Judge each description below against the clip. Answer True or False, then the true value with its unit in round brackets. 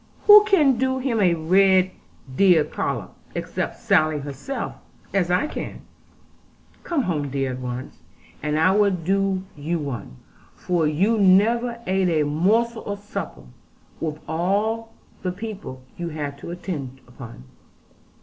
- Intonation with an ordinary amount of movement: False (5.8 semitones)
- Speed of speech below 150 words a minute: True (140 wpm)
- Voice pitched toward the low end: False (185 Hz)